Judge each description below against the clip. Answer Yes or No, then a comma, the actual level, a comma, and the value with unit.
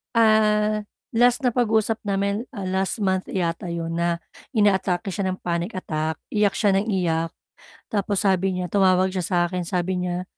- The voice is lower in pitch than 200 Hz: Yes, high, 190 Hz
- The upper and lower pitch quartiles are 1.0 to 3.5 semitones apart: Yes, average, 2.9 semitones